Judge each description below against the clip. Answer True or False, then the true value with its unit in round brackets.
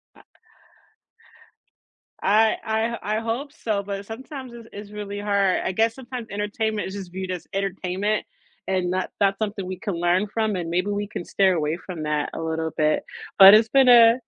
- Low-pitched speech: False (200 Hz)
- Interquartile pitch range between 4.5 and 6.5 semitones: False (3.1 semitones)